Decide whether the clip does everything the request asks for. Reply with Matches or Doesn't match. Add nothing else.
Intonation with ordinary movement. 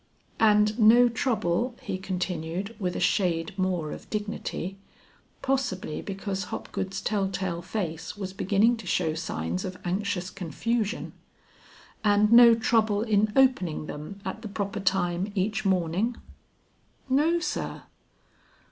Matches